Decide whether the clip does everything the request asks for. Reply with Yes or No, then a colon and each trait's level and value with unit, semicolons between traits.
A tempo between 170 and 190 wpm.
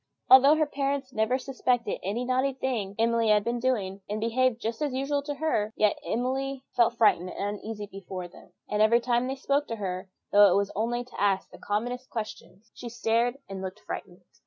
No: fast, 205 wpm